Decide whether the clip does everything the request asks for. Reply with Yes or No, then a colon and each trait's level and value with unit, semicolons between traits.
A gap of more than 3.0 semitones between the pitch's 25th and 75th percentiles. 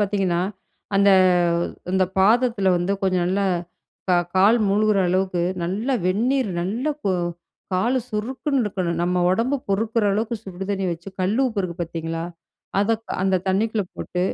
Yes: average, 3.4 semitones